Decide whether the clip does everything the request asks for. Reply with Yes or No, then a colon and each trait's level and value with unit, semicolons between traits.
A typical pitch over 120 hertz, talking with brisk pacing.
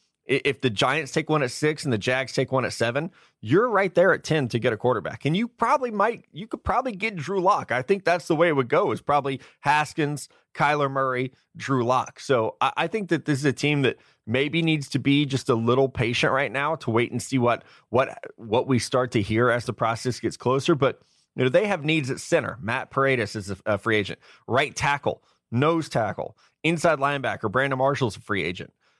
Yes: low, 135 Hz; fast, 230 wpm